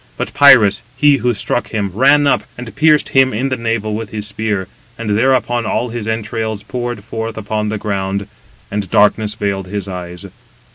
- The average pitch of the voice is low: Yes, low, 110 Hz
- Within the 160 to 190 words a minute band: Yes, average, 180 wpm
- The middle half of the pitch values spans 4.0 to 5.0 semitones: No, average, 3.0 semitones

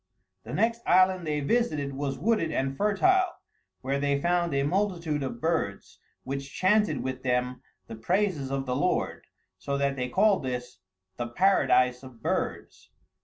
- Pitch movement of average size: No, wide, 6.2 semitones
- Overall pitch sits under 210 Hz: Yes, medium, 140 Hz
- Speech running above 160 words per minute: No, average, 155 wpm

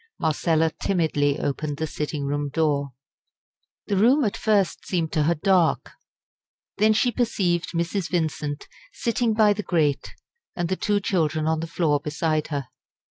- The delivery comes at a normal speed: Yes, average, 150 wpm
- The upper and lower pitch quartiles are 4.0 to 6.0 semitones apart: Yes, average, 4.6 semitones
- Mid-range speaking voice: Yes, medium, 165 Hz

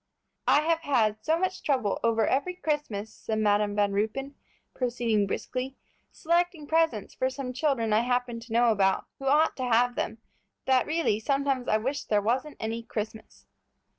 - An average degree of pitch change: Yes, average, 4.5 semitones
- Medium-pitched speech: No, high, 245 Hz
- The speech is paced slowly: No, average, 165 wpm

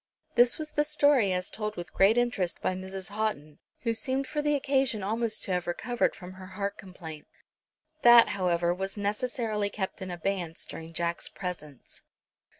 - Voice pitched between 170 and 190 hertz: No, high, 200 Hz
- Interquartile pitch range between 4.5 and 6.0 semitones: Yes, average, 4.9 semitones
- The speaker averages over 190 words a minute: No, average, 165 wpm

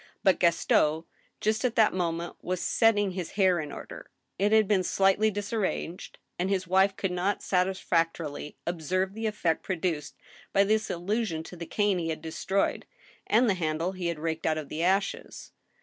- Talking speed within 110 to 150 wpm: No, average, 185 wpm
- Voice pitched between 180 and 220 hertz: Yes, medium, 185 Hz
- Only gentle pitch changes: No, average, 3.4 semitones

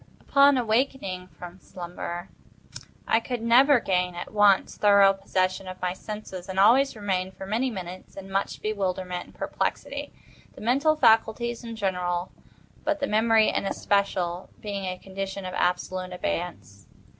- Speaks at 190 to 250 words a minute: No, average, 145 wpm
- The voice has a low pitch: No, high, 195 Hz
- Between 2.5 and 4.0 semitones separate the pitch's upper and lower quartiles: Yes, average, 3.5 semitones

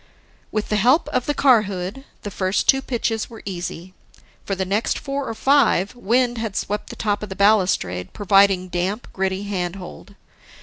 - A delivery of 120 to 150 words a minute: No, average, 175 wpm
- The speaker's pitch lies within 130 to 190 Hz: No, high, 205 Hz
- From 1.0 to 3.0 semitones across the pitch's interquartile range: No, average, 3.6 semitones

